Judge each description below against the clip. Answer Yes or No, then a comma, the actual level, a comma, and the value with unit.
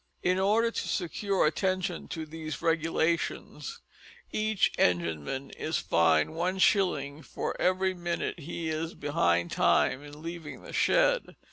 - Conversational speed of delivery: No, slow, 130 wpm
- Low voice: No, medium, 165 Hz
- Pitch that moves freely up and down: No, average, 4.2 semitones